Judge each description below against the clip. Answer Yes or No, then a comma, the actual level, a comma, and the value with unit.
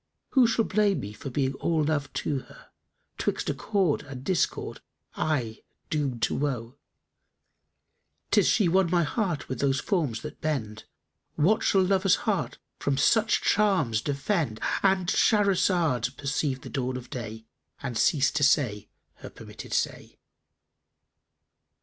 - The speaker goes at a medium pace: Yes, average, 145 wpm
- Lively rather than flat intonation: Yes, wide, 6.6 semitones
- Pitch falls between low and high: Yes, medium, 145 Hz